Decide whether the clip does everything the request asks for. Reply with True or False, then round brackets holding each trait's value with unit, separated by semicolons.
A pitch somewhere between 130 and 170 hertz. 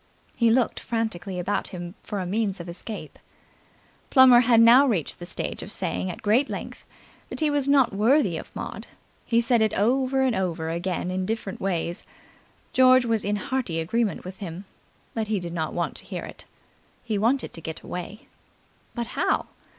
False (215 Hz)